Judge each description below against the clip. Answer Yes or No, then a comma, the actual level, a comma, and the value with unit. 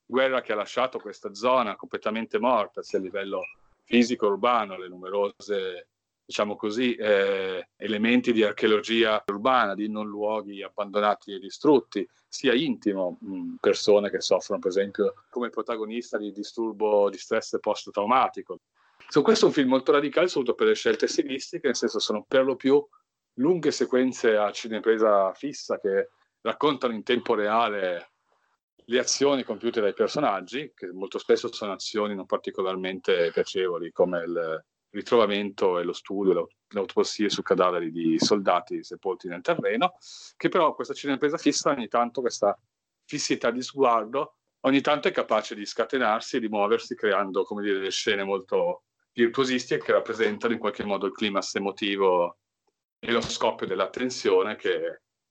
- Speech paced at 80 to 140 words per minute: No, average, 150 wpm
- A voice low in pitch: No, medium, 145 Hz